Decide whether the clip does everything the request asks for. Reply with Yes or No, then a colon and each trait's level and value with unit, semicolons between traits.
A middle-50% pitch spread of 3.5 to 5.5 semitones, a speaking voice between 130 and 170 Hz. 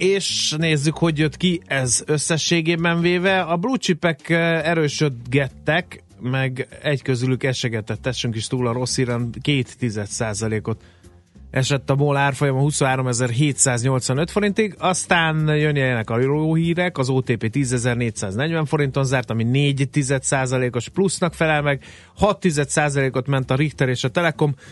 Yes: average, 4.1 semitones; medium, 140 Hz